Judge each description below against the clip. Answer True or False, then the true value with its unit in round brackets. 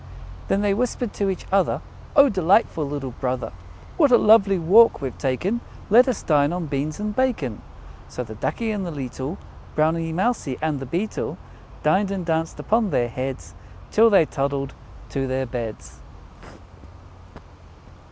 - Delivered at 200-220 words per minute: False (150 wpm)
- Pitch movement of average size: False (7.3 semitones)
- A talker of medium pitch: True (165 Hz)